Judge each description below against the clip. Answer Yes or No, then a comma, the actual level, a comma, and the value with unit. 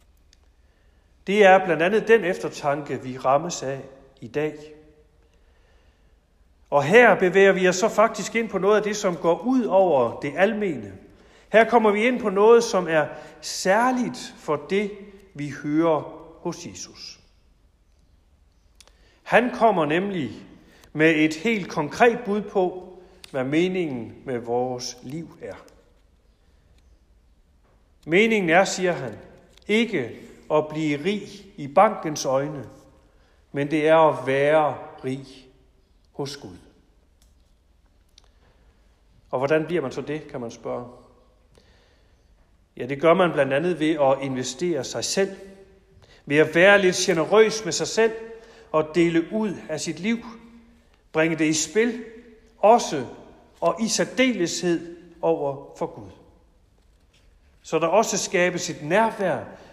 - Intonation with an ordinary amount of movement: No, wide, 9.0 semitones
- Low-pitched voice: No, medium, 155 Hz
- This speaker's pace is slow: Yes, slow, 130 wpm